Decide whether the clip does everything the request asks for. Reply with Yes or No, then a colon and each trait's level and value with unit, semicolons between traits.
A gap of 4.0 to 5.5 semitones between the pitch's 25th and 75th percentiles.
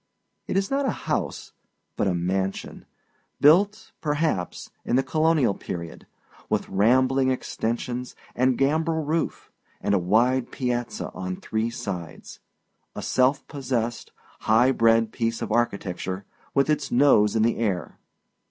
Yes: average, 4.9 semitones